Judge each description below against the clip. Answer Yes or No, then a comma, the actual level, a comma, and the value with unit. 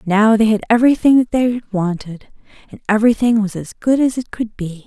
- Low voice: No, high, 220 Hz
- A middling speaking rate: Yes, average, 195 wpm